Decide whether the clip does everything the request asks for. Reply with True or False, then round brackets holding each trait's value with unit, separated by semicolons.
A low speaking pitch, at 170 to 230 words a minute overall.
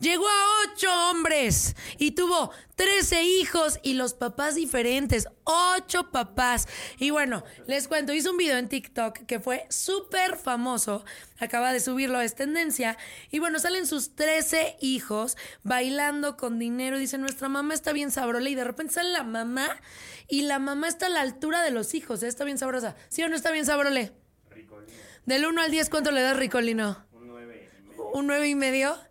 False (280 Hz; 180 wpm)